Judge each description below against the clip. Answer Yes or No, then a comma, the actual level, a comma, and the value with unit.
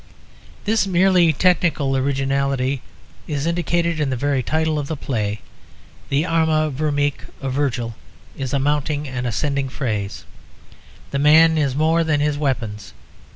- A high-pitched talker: No, medium, 145 Hz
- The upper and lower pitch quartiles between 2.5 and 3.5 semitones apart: Yes, average, 2.9 semitones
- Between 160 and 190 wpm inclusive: No, average, 140 wpm